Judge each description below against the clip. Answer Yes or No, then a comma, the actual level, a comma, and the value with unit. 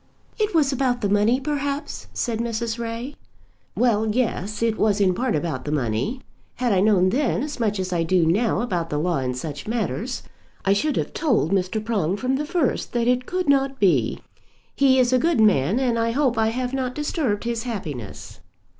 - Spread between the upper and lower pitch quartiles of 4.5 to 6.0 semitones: Yes, average, 5.2 semitones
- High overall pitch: Yes, high, 230 Hz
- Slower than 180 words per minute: No, average, 200 wpm